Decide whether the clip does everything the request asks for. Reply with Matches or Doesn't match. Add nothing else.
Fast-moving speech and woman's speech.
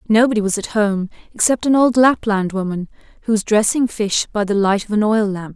Matches